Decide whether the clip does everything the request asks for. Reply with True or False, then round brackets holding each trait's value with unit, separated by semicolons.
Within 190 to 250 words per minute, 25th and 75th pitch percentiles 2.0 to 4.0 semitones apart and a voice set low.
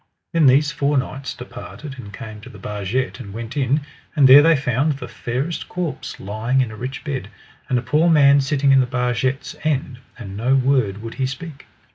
True (200 wpm; 3.2 semitones; 130 Hz)